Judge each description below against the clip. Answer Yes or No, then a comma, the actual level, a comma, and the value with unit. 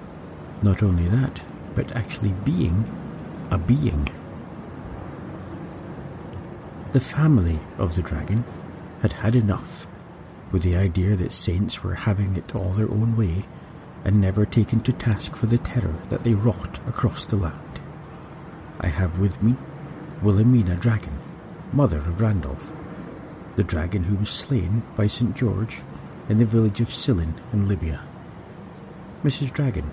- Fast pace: No, slow, 135 wpm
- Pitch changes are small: No, average, 4.3 semitones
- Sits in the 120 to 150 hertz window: No, low, 105 Hz